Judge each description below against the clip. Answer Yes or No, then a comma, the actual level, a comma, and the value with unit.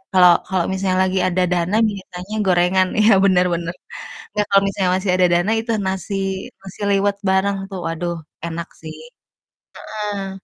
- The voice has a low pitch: No, high, 190 Hz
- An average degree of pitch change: No, narrow, 1.8 semitones